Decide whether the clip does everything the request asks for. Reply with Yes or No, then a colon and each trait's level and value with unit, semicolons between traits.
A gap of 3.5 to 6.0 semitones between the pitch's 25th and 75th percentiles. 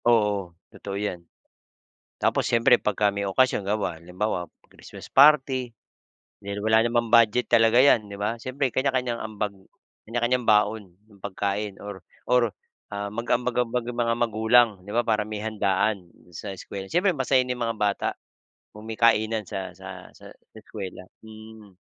No: average, 2.8 semitones